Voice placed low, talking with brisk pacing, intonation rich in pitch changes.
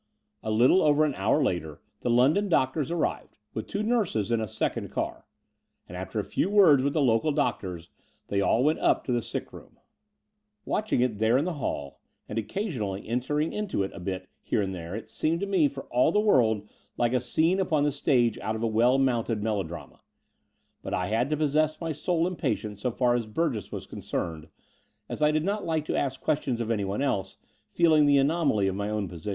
Yes: low, 125 Hz; fast, 210 wpm; wide, 6.5 semitones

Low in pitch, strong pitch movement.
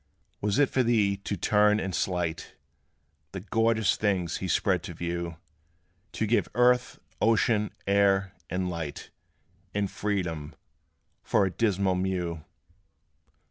No: low, 100 Hz; average, 3.1 semitones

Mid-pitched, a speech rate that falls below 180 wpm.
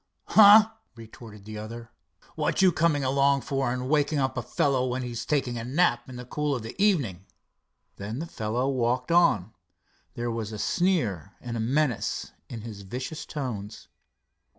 No: low, 125 Hz; average, 170 wpm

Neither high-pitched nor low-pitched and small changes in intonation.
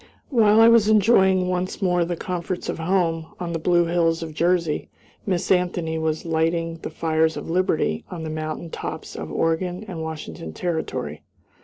Yes: medium, 170 Hz; narrow, 2.2 semitones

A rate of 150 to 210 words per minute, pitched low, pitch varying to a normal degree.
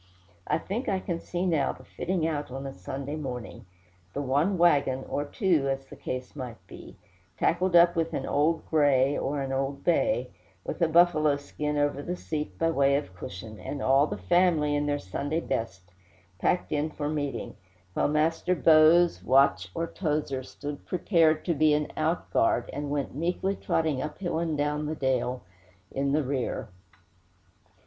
No: average, 170 wpm; medium, 150 Hz; average, 3.3 semitones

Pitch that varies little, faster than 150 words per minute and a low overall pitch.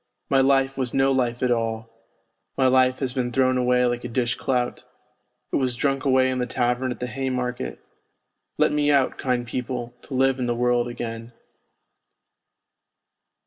Yes: narrow, 1.4 semitones; average, 170 wpm; low, 125 Hz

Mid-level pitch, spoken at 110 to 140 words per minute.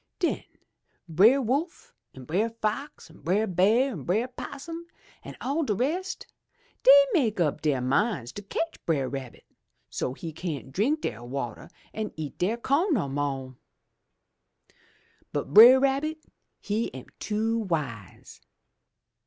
No: high, 210 Hz; slow, 135 wpm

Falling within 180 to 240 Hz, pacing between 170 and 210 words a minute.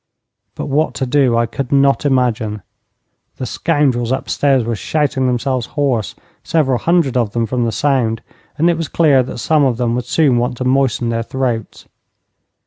No: low, 130 Hz; average, 175 wpm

